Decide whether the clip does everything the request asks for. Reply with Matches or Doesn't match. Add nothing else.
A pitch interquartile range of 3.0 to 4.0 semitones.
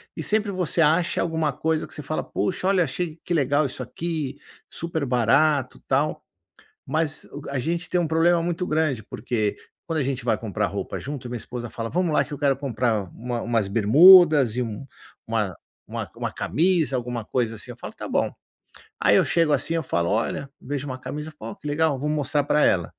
Doesn't match